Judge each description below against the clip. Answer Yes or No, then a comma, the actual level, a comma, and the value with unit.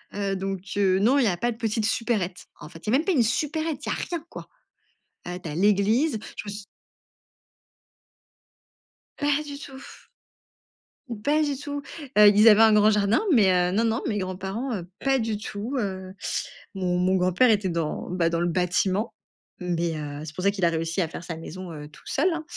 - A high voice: Yes, high, 205 Hz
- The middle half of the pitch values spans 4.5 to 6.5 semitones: Yes, average, 4.9 semitones